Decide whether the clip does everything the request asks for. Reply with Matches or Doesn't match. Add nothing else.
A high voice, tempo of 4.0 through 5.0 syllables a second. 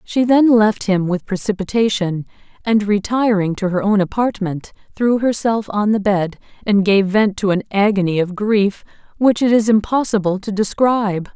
Matches